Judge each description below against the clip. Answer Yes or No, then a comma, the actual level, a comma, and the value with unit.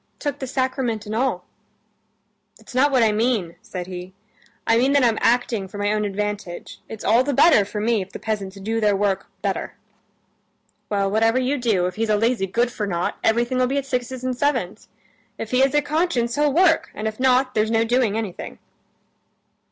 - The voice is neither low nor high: No, high, 225 Hz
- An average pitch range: Yes, average, 3.8 semitones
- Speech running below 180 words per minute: No, average, 200 wpm